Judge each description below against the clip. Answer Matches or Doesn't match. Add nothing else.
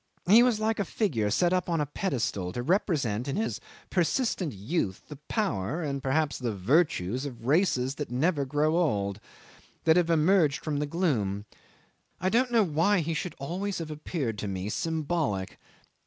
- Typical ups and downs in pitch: Doesn't match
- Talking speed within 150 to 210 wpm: Matches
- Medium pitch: Matches